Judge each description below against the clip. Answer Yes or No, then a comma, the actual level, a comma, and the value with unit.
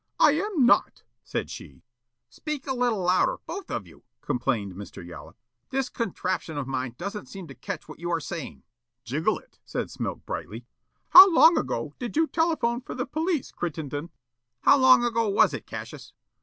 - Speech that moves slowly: No, average, 175 wpm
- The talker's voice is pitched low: No, high, 220 Hz